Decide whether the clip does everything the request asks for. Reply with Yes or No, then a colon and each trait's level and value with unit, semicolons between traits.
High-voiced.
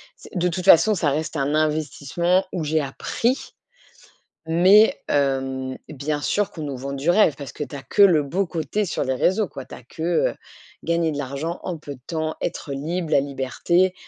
No: medium, 155 Hz